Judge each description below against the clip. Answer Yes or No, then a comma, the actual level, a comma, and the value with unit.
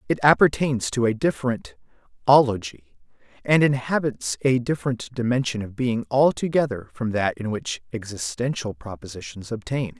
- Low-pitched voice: Yes, low, 120 Hz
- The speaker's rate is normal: No, slow, 125 wpm